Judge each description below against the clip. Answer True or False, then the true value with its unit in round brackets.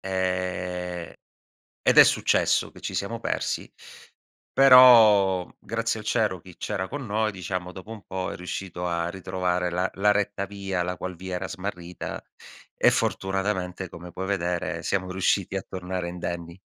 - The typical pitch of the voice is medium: False (95 Hz)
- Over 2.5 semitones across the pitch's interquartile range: False (1.8 semitones)